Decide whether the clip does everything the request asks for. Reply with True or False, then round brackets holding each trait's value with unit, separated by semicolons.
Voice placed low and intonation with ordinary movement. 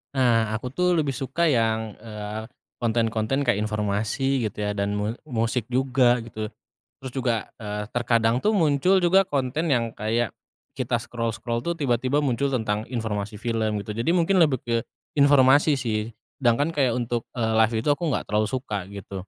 True (120 Hz; 3.7 semitones)